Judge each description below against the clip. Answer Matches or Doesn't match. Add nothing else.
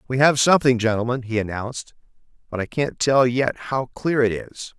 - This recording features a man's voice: Matches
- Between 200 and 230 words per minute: Doesn't match